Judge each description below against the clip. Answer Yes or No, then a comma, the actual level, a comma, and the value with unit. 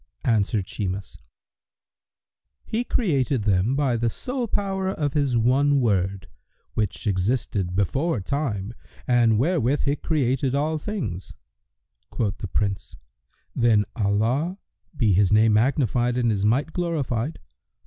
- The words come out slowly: Yes, slow, 120 wpm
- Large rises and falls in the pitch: Yes, wide, 5.7 semitones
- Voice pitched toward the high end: No, low, 120 Hz